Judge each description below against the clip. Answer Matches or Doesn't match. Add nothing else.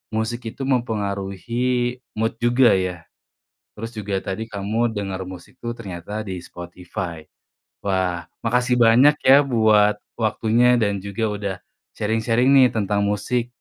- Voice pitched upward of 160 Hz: Doesn't match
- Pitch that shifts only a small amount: Doesn't match